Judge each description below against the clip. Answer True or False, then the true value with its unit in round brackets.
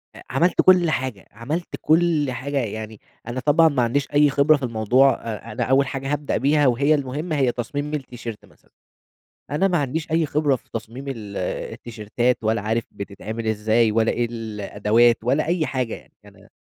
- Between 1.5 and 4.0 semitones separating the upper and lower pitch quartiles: False (4.4 semitones)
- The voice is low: True (130 Hz)